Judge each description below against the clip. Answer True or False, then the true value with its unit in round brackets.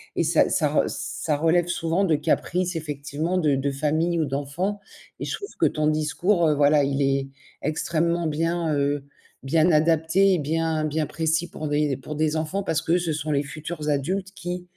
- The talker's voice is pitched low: False (155 Hz)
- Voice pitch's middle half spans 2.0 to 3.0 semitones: True (2.6 semitones)